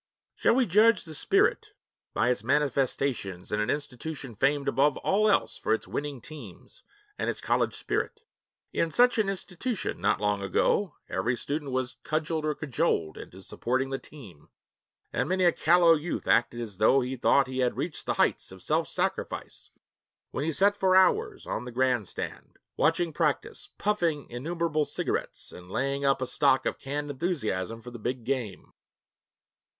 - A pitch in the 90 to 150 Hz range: Yes, medium, 140 Hz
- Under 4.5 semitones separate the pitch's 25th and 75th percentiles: No, wide, 5.5 semitones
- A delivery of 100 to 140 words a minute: No, average, 165 wpm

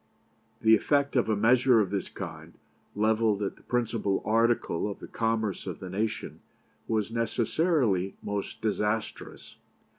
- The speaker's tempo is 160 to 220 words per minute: No, average, 140 wpm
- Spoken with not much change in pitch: Yes, narrow, 2.2 semitones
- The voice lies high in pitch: No, low, 110 Hz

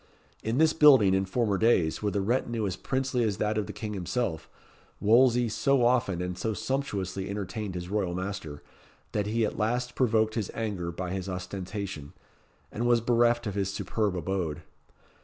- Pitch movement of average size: Yes, average, 4.0 semitones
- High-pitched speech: No, low, 105 Hz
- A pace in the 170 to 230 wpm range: Yes, average, 175 wpm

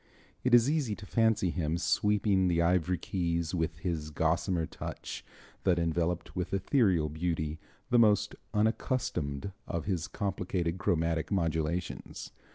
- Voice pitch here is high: No, very low, 90 Hz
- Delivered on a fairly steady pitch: No, average, 3.4 semitones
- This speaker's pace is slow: Yes, slow, 130 wpm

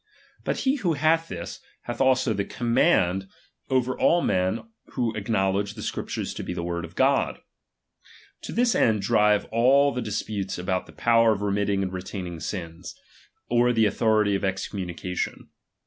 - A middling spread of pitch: Yes, average, 4.4 semitones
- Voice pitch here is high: No, low, 105 Hz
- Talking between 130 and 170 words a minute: Yes, average, 165 wpm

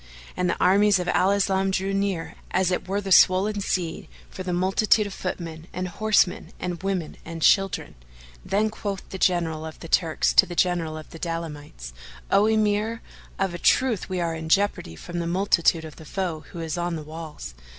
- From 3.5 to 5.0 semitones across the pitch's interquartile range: No, average, 3.0 semitones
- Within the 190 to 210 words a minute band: Yes, average, 195 wpm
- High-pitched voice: No, medium, 180 Hz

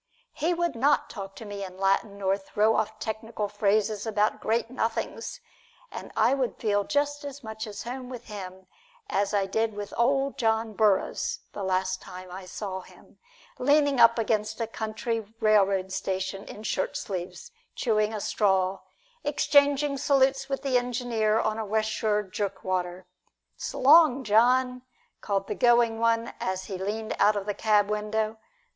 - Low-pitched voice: No, high, 215 Hz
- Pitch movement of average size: Yes, average, 3.4 semitones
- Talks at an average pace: Yes, average, 165 wpm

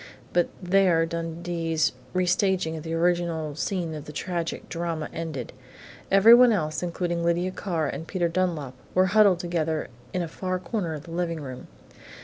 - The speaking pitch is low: No, medium, 170 Hz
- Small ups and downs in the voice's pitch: Yes, narrow, 2.2 semitones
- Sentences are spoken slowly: No, average, 155 wpm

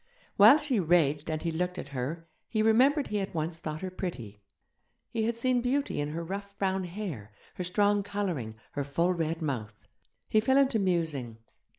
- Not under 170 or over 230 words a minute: Yes, average, 185 wpm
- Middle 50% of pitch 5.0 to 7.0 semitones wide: Yes, wide, 5.4 semitones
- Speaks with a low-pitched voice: No, medium, 180 Hz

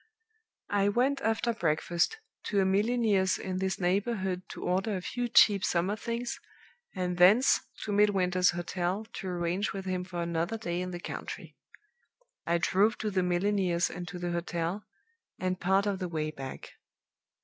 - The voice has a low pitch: No, medium, 185 Hz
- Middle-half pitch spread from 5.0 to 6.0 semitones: No, average, 2.8 semitones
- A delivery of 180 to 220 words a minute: No, average, 160 wpm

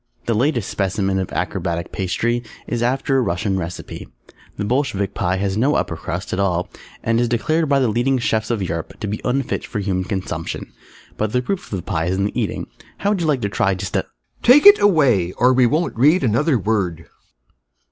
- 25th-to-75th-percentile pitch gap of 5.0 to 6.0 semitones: Yes, wide, 5.6 semitones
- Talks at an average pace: No, fast, 210 wpm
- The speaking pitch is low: Yes, low, 110 Hz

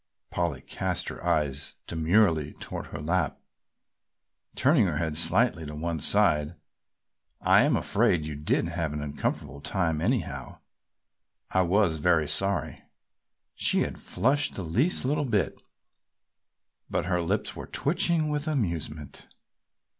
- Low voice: Yes, very low, 85 Hz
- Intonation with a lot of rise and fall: Yes, wide, 5.9 semitones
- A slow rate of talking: Yes, slow, 130 wpm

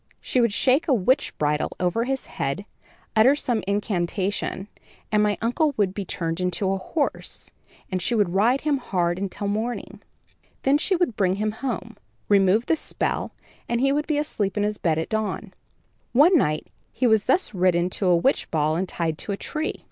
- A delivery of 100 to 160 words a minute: No, average, 185 wpm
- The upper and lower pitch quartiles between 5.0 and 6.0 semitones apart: Yes, wide, 5.6 semitones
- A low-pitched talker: No, high, 205 Hz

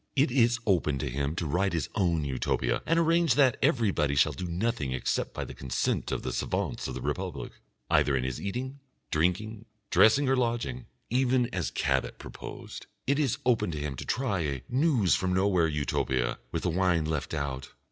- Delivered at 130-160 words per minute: No, average, 190 wpm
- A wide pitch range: Yes, wide, 8.6 semitones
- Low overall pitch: Yes, very low, 90 Hz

